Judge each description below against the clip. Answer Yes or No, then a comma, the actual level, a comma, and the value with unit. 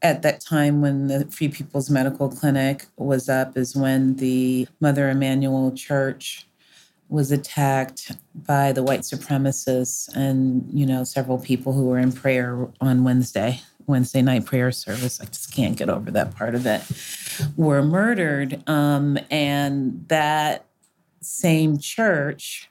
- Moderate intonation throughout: No, narrow, 2.0 semitones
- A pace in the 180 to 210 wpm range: No, average, 145 wpm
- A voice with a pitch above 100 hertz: Yes, low, 135 Hz